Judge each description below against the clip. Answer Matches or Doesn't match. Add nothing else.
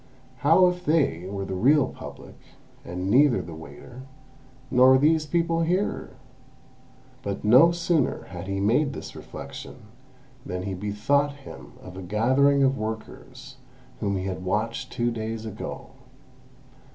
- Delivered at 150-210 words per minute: Doesn't match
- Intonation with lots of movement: Matches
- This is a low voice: Matches